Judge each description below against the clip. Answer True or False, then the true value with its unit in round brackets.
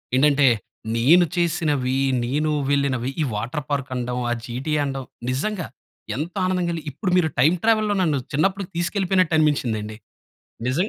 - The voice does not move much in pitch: False (5.1 semitones)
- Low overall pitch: False (150 Hz)